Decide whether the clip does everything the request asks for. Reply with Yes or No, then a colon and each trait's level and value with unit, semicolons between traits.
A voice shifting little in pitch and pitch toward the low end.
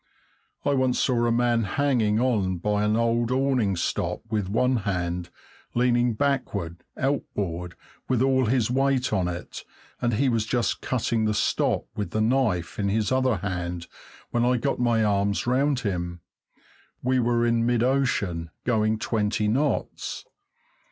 No: average, 3.9 semitones; low, 115 Hz